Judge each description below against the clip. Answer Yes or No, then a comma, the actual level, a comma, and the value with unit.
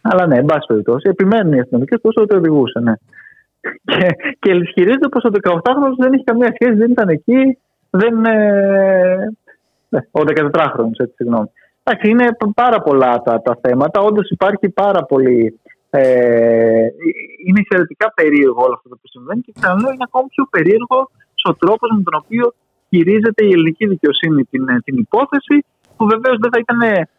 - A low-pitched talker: No, high, 195 Hz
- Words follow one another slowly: No, average, 165 wpm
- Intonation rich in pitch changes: Yes, wide, 8.6 semitones